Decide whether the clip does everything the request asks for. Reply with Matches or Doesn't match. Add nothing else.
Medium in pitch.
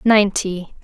Doesn't match